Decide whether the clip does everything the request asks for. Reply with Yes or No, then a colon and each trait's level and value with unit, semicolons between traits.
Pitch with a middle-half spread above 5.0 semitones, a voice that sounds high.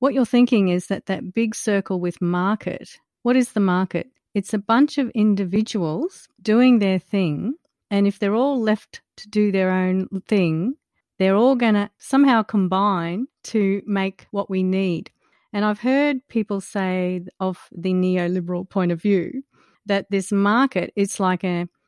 No: average, 3.4 semitones; high, 200 Hz